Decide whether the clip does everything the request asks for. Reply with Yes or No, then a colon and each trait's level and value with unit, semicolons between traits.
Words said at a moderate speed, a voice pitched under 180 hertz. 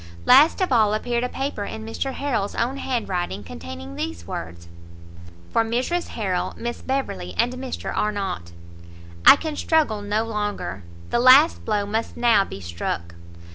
No: average, 155 wpm; high, 215 Hz